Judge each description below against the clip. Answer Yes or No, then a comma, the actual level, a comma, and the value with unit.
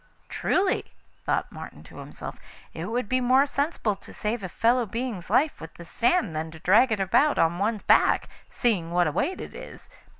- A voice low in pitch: No, high, 220 Hz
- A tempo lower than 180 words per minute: No, average, 195 wpm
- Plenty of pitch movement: Yes, wide, 6.3 semitones